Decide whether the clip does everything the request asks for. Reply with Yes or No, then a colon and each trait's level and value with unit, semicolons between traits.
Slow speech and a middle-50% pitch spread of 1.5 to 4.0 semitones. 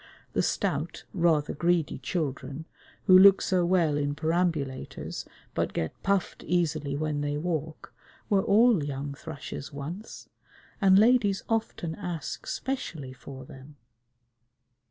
No: slow, 120 wpm; average, 4.5 semitones